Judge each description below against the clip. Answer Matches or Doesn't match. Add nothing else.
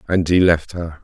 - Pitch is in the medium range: Doesn't match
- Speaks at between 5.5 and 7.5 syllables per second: Doesn't match